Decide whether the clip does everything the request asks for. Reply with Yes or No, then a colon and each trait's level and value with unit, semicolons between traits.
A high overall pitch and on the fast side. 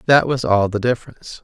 No: low, 115 Hz; fast, 210 wpm